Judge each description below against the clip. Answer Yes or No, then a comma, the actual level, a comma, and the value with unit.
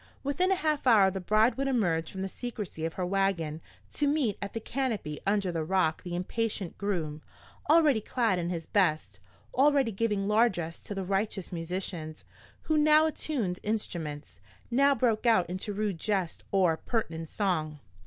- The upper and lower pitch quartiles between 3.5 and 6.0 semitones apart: Yes, average, 5.2 semitones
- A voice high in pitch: Yes, high, 195 Hz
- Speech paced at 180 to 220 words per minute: No, average, 165 wpm